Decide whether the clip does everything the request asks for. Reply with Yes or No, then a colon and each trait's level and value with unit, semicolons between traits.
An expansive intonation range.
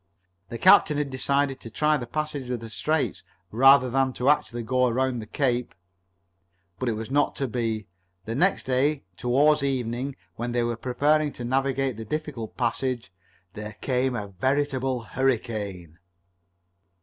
No: average, 3.1 semitones